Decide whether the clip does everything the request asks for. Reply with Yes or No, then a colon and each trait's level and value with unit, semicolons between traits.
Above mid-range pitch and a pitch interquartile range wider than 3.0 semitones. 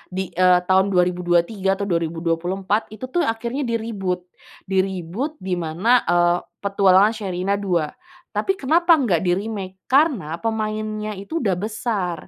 Yes: high, 195 Hz; average, 3.6 semitones